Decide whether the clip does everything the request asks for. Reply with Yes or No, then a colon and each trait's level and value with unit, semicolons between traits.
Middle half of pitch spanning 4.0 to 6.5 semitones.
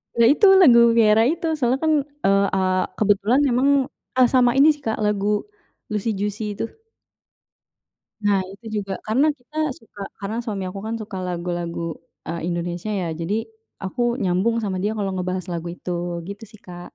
Yes: average, 4.3 semitones